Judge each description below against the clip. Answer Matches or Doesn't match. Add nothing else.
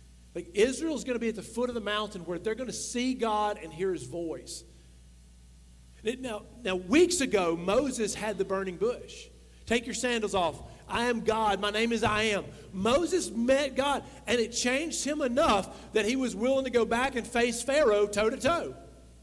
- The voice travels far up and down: Doesn't match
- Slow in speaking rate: Doesn't match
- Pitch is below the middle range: Doesn't match